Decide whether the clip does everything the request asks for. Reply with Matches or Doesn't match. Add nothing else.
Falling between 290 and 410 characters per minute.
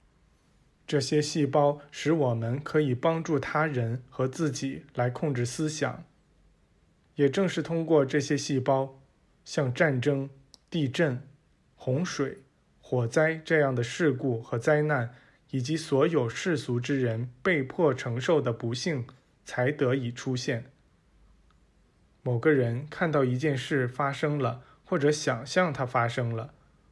Doesn't match